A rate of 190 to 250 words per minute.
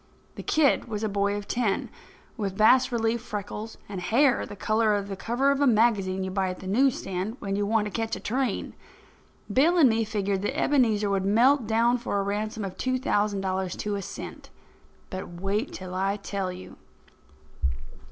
Yes: average, 195 wpm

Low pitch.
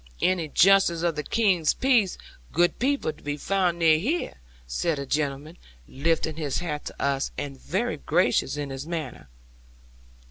No: medium, 160 Hz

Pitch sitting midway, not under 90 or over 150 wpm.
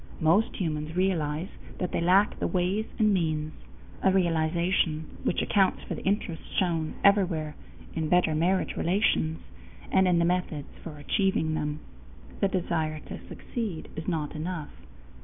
Yes: medium, 170 Hz; average, 145 wpm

